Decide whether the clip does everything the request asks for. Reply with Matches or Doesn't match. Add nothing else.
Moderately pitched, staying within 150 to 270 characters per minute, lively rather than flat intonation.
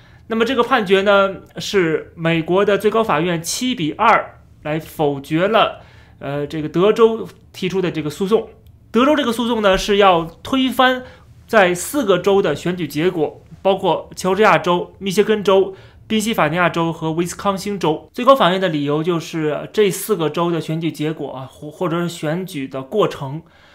Doesn't match